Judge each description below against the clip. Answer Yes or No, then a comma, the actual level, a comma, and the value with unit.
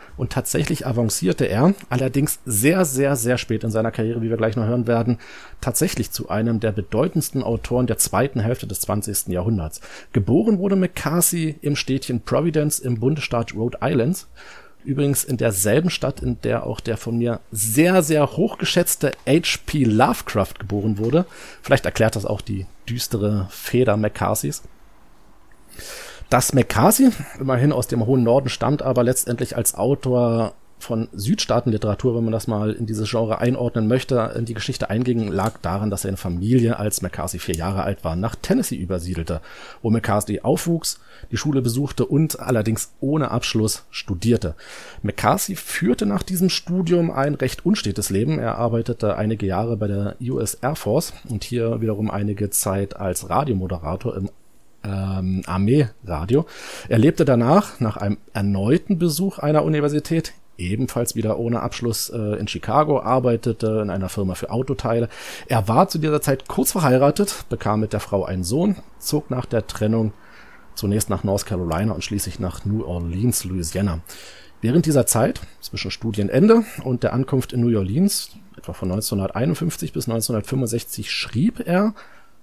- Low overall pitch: Yes, low, 115 Hz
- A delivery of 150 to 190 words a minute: Yes, average, 155 wpm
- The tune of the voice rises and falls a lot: No, average, 4.7 semitones